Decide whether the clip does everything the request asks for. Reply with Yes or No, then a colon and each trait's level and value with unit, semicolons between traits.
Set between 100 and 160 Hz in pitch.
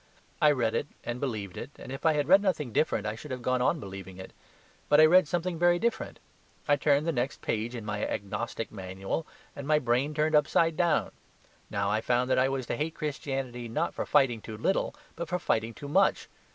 Yes: low, 135 Hz